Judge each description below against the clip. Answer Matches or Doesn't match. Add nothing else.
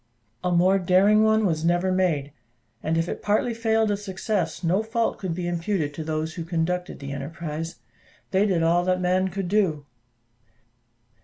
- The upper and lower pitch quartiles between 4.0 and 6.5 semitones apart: Doesn't match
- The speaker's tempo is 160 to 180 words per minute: Matches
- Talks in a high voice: Doesn't match